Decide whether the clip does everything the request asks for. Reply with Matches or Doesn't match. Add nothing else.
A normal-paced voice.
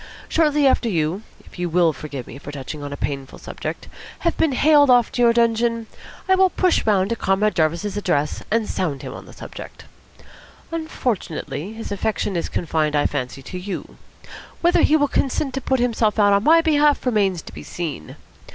Matches